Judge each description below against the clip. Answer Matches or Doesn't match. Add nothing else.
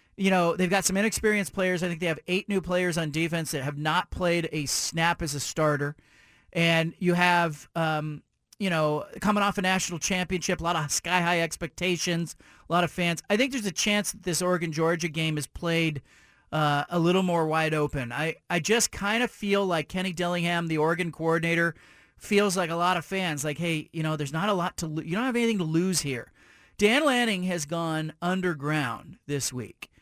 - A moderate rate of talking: Doesn't match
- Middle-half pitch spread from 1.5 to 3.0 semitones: Matches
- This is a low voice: Doesn't match